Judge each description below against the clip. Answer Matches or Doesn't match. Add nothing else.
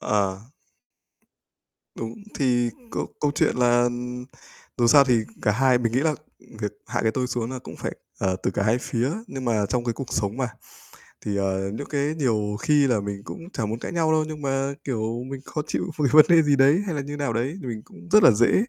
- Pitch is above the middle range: Doesn't match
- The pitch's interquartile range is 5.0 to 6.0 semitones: Doesn't match